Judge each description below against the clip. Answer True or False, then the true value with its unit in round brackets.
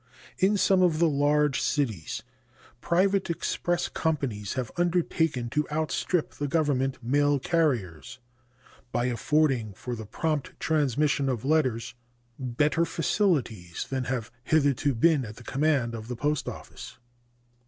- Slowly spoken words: True (130 wpm)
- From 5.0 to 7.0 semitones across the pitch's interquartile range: False (4.6 semitones)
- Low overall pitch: False (145 Hz)